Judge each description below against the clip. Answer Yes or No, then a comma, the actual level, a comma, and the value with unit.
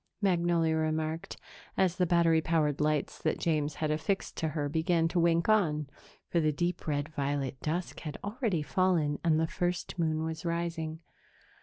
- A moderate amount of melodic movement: No, narrow, 2.1 semitones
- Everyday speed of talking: Yes, average, 165 wpm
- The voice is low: No, medium, 160 Hz